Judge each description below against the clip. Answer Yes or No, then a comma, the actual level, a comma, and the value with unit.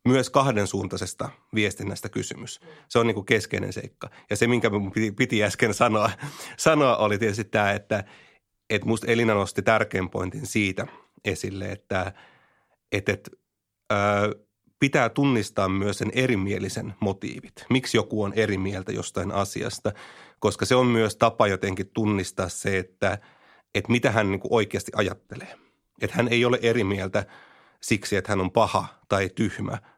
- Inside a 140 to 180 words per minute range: Yes, average, 150 wpm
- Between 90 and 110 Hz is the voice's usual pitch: Yes, low, 105 Hz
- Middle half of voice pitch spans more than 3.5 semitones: No, average, 3.0 semitones